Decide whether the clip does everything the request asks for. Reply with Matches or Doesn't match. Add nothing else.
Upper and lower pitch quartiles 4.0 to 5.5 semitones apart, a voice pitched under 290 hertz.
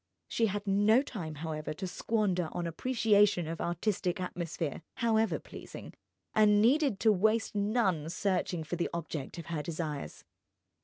Matches